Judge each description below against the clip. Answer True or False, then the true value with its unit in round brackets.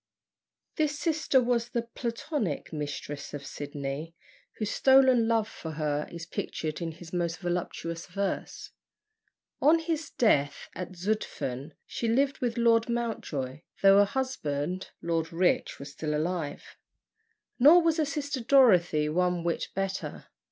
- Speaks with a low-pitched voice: False (185 Hz)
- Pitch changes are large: True (7.5 semitones)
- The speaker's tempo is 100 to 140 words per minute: True (135 wpm)